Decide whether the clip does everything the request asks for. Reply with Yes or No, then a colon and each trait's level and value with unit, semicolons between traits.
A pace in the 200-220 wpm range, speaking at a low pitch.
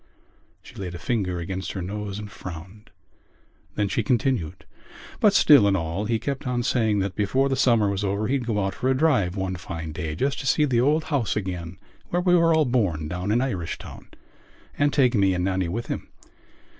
Yes: fast, 205 wpm; low, 105 Hz